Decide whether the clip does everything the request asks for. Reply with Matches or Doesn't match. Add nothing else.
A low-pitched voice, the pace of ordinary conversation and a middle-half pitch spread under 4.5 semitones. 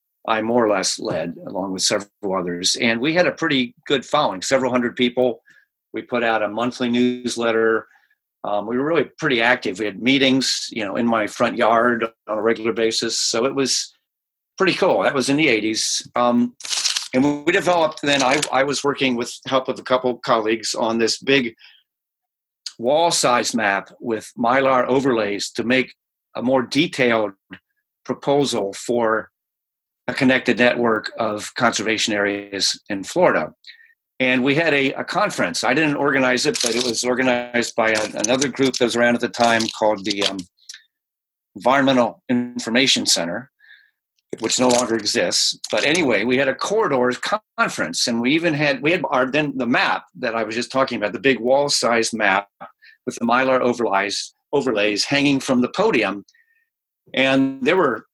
Matches